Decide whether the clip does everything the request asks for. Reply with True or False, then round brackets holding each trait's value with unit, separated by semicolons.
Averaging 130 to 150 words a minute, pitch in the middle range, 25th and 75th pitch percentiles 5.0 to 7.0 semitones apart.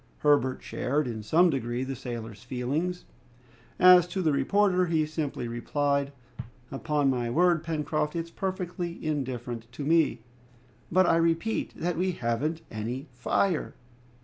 True (135 wpm; 150 Hz; 5.3 semitones)